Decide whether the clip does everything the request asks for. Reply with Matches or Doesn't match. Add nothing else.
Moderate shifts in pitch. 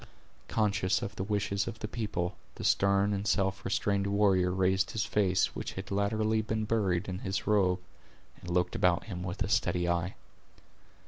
Doesn't match